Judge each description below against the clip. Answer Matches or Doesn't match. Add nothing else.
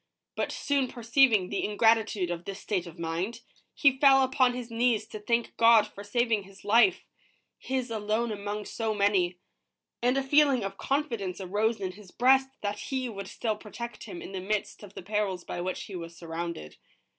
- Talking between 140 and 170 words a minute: Doesn't match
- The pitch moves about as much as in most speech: Matches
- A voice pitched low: Doesn't match